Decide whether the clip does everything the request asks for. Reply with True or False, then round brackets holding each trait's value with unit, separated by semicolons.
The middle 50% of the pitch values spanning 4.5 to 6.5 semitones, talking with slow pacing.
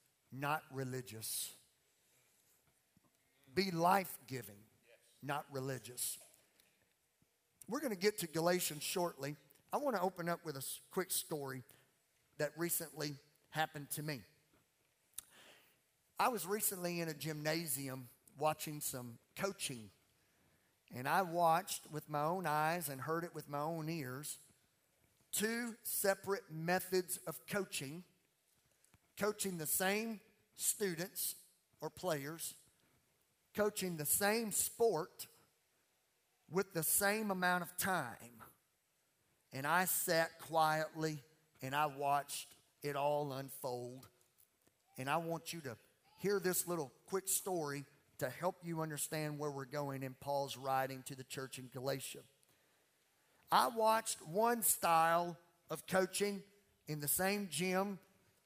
True (4.9 semitones; 120 wpm)